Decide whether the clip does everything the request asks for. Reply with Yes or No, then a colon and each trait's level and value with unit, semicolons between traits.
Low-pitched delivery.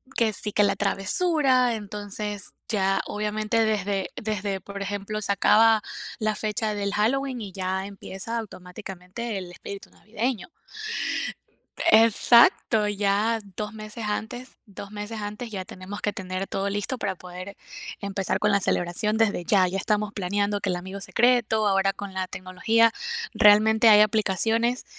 No: high, 205 Hz